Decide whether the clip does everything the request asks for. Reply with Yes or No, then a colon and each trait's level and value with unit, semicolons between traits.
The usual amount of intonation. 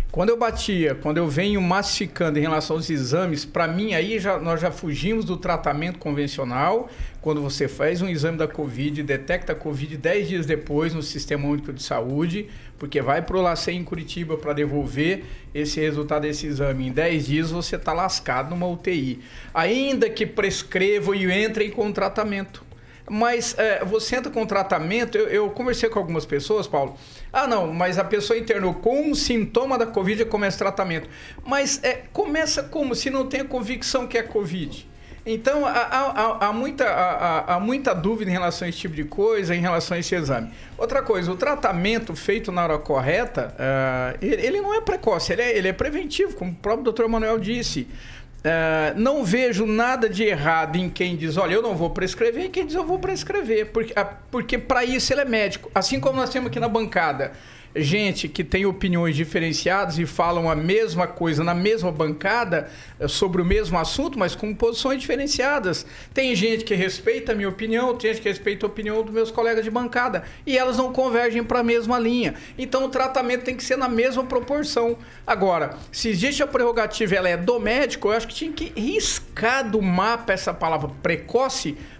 No: wide, 6.4 semitones